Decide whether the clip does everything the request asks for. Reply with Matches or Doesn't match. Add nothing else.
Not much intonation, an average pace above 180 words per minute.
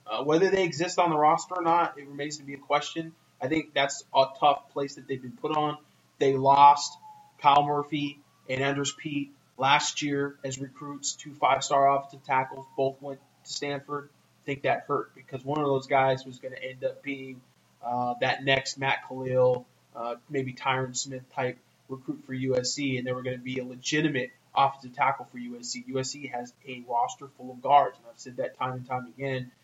Matches